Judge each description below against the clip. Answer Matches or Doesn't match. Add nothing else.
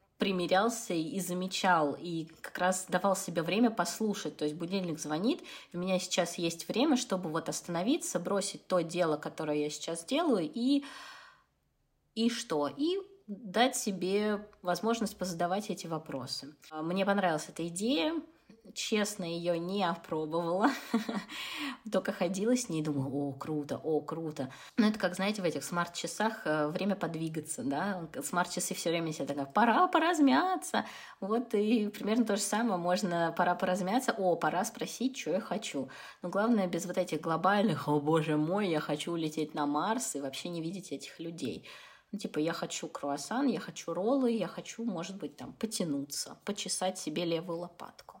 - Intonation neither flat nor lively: Matches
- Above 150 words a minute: Matches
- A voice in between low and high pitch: Matches